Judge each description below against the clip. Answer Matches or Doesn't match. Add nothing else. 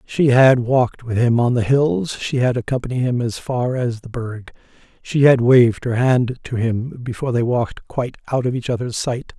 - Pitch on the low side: Matches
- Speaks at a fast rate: Matches